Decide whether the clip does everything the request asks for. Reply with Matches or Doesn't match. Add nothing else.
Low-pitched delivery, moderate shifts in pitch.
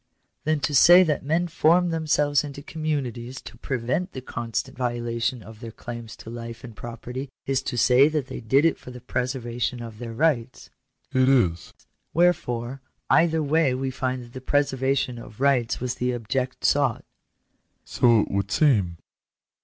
Matches